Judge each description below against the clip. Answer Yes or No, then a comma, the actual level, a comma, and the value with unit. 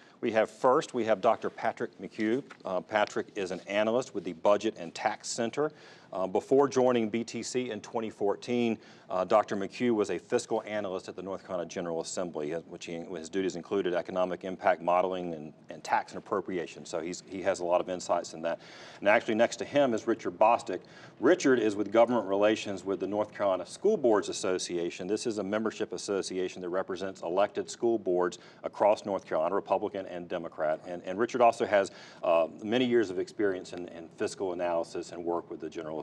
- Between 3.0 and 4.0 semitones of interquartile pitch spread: No, average, 4.6 semitones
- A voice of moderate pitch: No, low, 100 Hz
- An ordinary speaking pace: Yes, average, 195 wpm